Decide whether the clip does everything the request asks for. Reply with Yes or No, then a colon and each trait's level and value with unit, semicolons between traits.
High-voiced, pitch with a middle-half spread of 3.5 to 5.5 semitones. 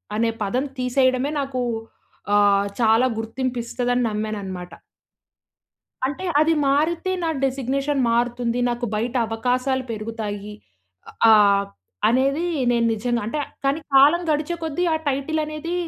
Yes: very high, 250 Hz; average, 3.8 semitones